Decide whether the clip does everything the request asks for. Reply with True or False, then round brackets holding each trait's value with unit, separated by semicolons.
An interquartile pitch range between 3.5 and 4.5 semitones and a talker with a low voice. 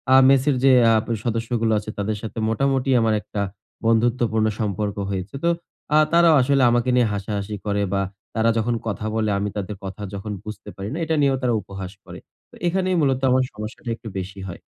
True (3.8 semitones; 110 Hz)